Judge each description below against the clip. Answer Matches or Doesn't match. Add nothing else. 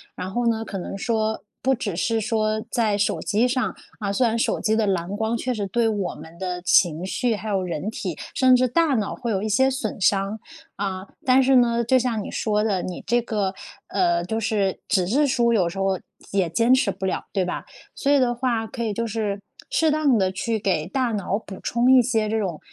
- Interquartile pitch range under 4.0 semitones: Matches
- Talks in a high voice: Matches